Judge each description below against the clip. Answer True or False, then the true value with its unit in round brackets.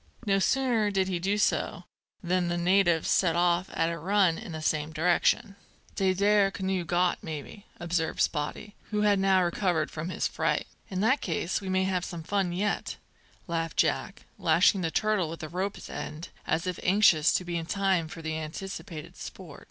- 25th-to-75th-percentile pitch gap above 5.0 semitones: False (3.0 semitones)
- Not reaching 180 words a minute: False (185 wpm)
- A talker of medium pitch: True (180 Hz)